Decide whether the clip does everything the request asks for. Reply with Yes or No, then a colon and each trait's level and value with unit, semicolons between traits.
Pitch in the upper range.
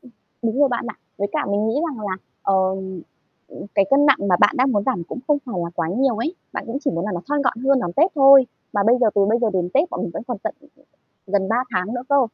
Yes: high, 225 Hz